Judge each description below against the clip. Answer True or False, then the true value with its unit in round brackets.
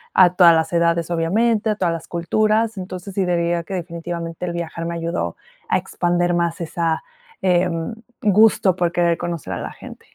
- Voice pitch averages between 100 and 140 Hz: False (175 Hz)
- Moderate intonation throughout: False (1.7 semitones)